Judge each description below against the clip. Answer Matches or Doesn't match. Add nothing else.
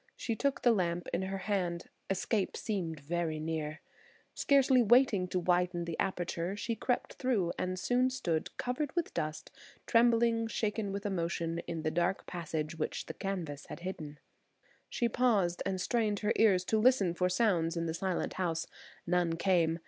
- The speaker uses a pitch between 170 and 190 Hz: Matches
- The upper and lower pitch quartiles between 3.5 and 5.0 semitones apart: Matches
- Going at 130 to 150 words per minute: Doesn't match